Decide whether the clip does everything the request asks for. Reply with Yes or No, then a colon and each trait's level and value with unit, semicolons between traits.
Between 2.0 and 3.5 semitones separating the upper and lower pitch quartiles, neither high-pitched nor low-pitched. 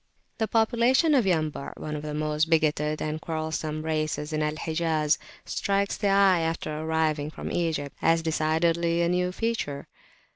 Yes: average, 2.7 semitones; medium, 160 Hz